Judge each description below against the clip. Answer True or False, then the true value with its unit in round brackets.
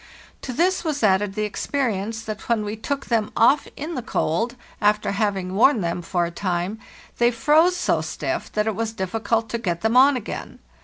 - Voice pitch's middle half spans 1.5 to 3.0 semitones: False (3.9 semitones)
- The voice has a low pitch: False (220 Hz)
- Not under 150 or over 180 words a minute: False (195 wpm)